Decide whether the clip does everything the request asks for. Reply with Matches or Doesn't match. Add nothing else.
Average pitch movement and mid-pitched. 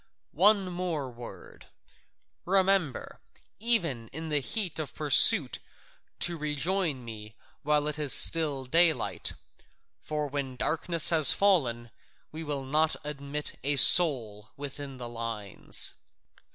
Matches